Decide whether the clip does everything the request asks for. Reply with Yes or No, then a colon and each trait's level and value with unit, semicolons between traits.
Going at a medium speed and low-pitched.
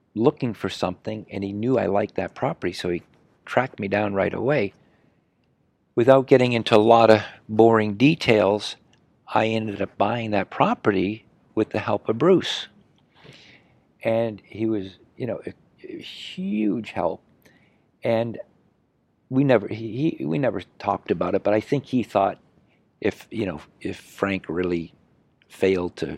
Yes: average, 155 wpm; low, 110 Hz